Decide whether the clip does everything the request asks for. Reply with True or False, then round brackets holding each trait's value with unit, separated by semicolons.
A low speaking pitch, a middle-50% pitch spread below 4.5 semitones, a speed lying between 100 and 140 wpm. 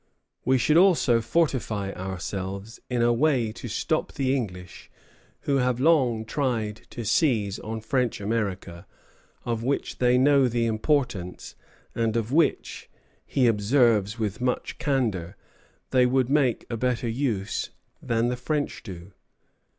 True (120 Hz; 3.7 semitones; 135 wpm)